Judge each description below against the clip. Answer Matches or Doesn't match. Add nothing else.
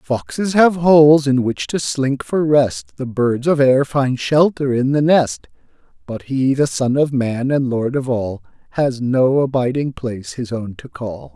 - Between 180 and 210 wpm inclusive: Matches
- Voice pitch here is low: Matches